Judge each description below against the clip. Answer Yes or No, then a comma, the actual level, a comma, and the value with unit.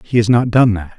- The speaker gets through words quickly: Yes, fast, 305 wpm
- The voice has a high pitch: No, low, 110 Hz